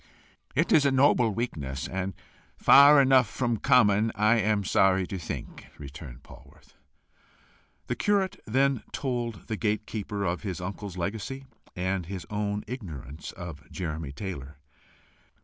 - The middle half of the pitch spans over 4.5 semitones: Yes, average, 5.1 semitones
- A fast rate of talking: No, slow, 135 wpm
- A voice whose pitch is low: Yes, low, 100 Hz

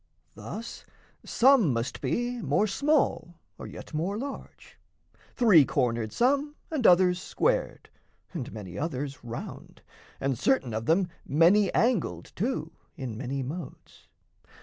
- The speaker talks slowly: Yes, slow, 125 wpm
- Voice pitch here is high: No, medium, 175 Hz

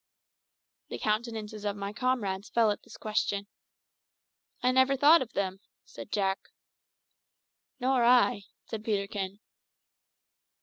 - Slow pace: Yes, slow, 115 wpm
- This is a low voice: No, high, 215 Hz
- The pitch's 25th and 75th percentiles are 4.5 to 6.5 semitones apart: No, average, 3.6 semitones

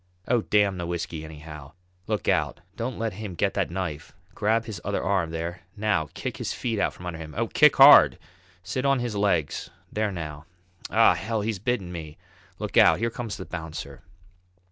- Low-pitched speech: Yes, very low, 95 Hz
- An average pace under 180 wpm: No, average, 185 wpm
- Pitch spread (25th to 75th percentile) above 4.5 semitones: Yes, average, 5.0 semitones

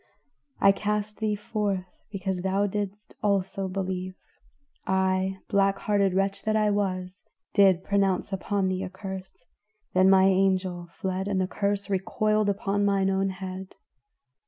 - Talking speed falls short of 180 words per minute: Yes, average, 140 wpm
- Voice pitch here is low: No, high, 195 Hz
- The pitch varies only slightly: Yes, narrow, 1.4 semitones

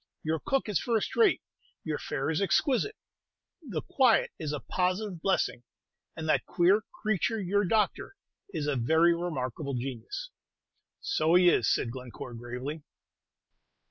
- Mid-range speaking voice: Yes, medium, 170 Hz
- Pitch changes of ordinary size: No, wide, 6.7 semitones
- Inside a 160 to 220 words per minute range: No, average, 140 wpm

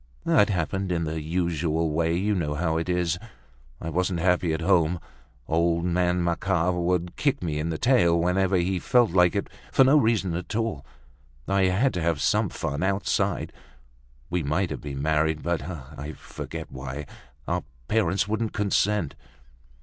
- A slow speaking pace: No, average, 160 wpm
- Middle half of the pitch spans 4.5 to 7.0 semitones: No, average, 3.1 semitones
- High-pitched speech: No, very low, 85 Hz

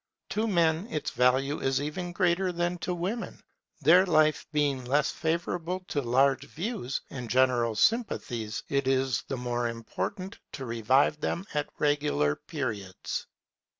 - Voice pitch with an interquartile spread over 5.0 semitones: Yes, wide, 5.6 semitones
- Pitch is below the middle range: No, medium, 145 Hz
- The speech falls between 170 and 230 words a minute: No, average, 140 wpm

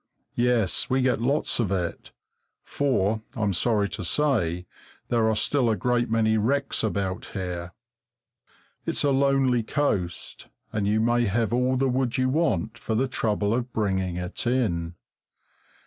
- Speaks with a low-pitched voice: Yes, low, 115 Hz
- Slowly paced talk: No, average, 150 wpm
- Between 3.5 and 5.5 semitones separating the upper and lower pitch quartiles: Yes, average, 4.3 semitones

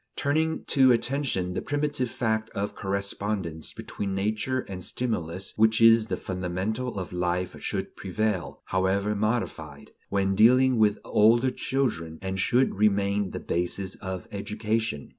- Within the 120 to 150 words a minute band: Yes, slow, 135 wpm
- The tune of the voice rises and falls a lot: No, average, 3.6 semitones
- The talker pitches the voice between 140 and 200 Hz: No, low, 105 Hz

